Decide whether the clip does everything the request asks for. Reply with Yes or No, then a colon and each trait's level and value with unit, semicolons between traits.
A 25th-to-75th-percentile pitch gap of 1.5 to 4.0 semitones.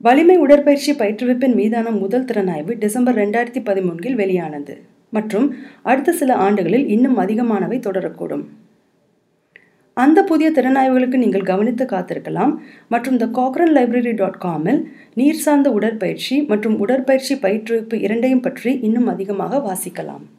No: average, 4.6 semitones